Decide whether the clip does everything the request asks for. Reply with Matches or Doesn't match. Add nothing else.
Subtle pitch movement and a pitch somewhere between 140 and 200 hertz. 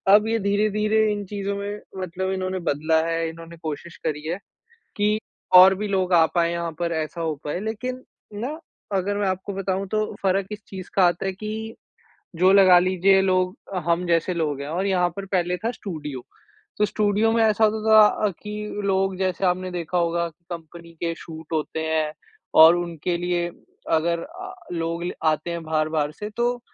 Doesn't match